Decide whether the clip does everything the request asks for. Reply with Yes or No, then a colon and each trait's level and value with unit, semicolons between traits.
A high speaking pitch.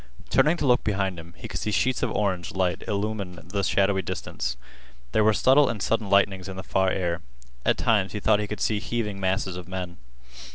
No: low, 100 Hz